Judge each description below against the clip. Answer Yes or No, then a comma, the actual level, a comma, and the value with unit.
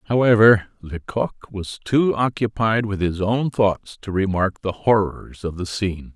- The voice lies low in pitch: Yes, low, 100 Hz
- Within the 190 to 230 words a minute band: No, average, 155 wpm